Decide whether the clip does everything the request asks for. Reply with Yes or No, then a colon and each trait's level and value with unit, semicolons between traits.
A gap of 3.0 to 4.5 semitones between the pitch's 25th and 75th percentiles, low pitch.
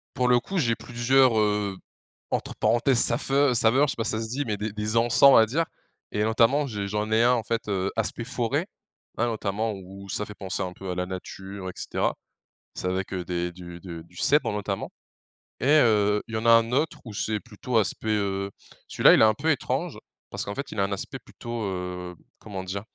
Yes: average, 3.5 semitones; low, 110 Hz